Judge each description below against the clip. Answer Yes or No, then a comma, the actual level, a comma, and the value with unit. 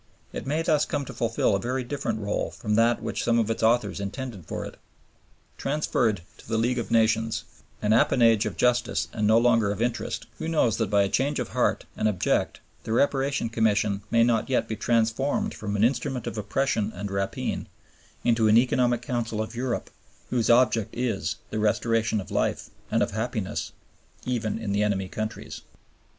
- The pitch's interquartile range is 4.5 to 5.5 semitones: No, narrow, 2.5 semitones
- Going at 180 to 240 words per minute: Yes, average, 185 wpm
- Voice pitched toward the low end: Yes, low, 115 Hz